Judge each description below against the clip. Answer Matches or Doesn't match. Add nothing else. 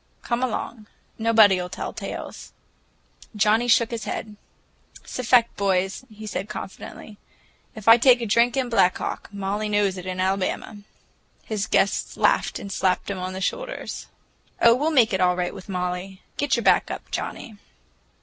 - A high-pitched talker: Matches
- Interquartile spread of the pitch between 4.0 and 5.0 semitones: Doesn't match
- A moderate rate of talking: Matches